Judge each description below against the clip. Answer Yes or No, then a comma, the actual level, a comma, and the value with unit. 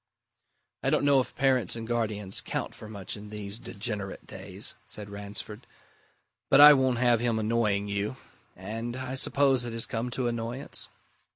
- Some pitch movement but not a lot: Yes, average, 3.2 semitones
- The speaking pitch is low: Yes, low, 115 Hz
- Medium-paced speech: Yes, average, 165 wpm